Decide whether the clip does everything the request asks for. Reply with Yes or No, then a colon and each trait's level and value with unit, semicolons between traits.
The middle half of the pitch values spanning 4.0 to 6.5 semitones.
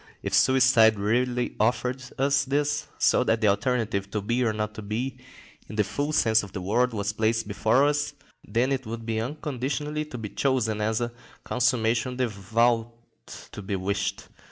No: average, 3.3 semitones